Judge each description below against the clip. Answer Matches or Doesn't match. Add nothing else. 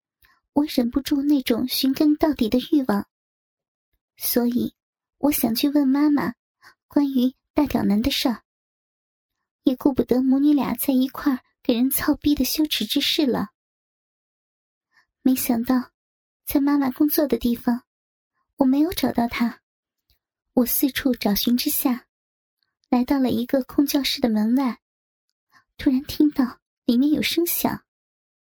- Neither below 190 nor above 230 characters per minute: Matches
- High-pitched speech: Matches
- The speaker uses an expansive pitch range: Doesn't match